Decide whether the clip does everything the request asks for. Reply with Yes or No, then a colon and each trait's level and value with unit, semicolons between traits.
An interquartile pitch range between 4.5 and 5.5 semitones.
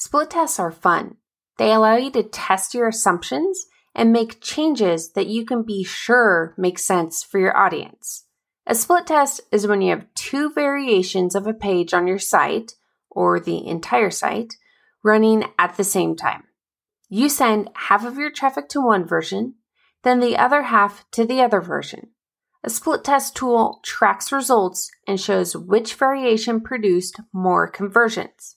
Yes: average, 5.2 semitones